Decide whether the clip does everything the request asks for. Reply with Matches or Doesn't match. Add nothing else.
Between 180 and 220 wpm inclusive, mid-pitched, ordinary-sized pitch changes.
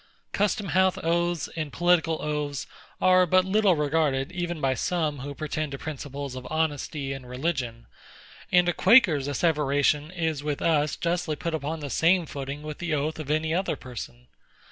Doesn't match